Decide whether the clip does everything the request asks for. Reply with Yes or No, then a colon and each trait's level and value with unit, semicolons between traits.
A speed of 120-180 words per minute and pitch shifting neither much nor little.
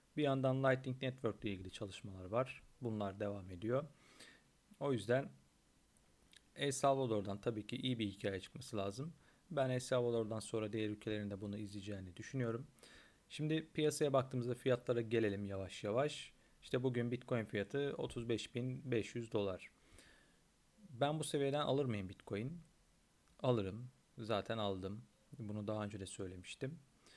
Yes: average, 125 wpm; average, 4.3 semitones